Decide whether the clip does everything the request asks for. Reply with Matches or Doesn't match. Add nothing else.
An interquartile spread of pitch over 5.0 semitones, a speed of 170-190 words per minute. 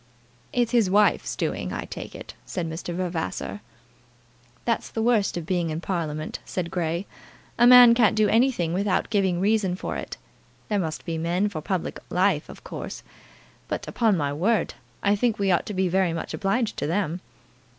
Doesn't match